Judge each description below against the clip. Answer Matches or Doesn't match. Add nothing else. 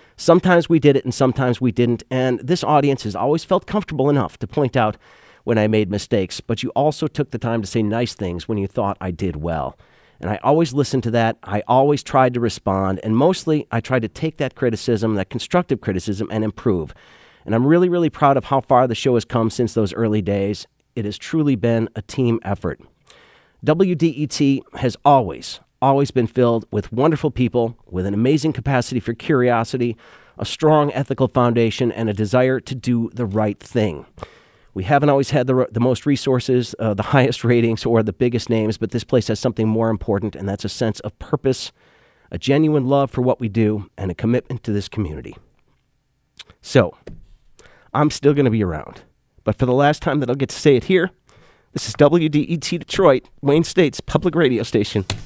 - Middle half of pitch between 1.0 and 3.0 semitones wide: Doesn't match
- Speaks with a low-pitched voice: Matches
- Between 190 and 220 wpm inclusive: Matches